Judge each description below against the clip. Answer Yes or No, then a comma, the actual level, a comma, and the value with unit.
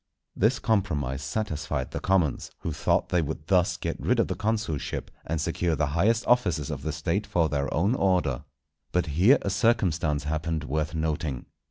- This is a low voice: Yes, very low, 80 Hz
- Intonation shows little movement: No, average, 4.7 semitones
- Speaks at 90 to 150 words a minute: No, average, 175 wpm